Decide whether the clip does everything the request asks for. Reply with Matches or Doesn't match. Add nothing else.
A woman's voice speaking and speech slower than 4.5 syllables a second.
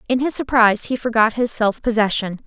Doesn't match